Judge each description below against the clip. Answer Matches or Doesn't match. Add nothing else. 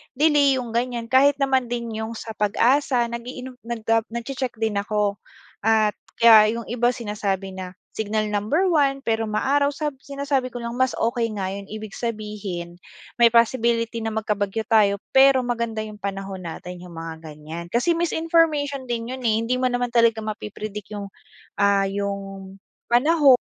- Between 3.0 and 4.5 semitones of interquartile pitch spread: Matches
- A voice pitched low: Doesn't match